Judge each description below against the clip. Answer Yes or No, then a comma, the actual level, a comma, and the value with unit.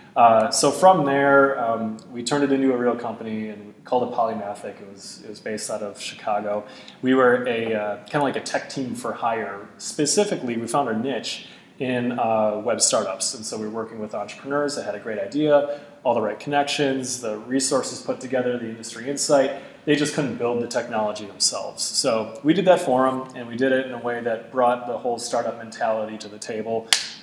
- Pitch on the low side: Yes, low, 125 Hz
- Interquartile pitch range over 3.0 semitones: Yes, average, 4.0 semitones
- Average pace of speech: No, fast, 215 wpm